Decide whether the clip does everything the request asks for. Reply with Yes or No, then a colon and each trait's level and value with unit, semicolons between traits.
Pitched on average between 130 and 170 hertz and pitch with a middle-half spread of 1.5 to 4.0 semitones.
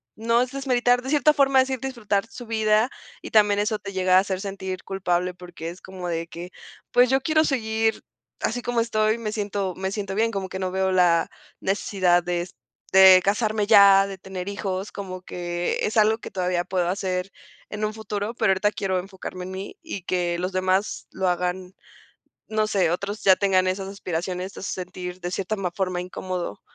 No: high, 195 Hz; average, 2.9 semitones